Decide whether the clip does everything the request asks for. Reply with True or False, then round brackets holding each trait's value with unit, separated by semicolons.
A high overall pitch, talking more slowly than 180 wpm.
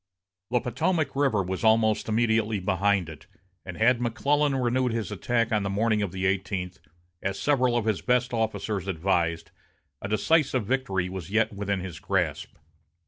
False (110 Hz; 160 wpm)